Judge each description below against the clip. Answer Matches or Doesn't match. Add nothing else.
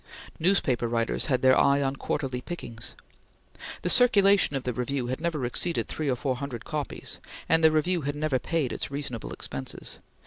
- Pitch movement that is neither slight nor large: Matches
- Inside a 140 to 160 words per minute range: Doesn't match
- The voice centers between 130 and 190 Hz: Matches